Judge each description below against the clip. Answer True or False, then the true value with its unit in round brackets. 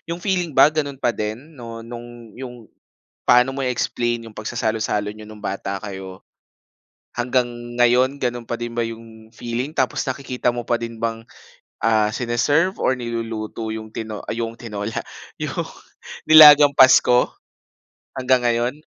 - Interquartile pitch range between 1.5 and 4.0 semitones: True (2.4 semitones)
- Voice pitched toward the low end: True (120 Hz)